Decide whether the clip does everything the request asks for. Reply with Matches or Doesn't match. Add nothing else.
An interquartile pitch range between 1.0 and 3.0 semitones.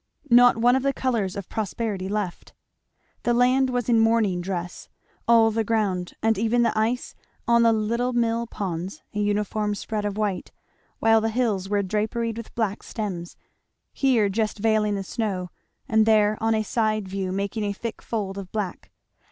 Matches